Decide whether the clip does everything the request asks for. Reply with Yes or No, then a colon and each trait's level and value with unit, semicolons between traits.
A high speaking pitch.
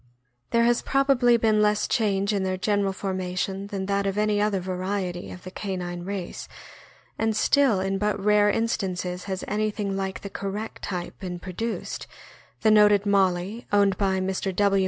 Yes: high, 200 Hz